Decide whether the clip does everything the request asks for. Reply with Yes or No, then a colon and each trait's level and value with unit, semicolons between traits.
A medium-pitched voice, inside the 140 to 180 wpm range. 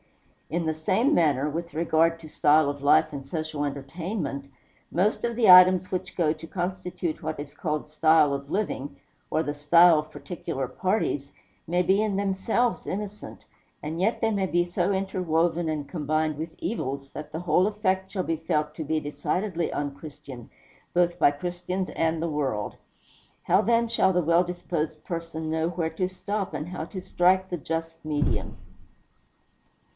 Yes: medium, 165 Hz; average, 170 wpm